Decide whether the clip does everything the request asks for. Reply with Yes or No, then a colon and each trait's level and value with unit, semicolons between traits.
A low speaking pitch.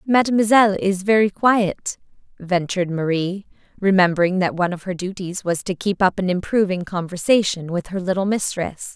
No: high, 190 Hz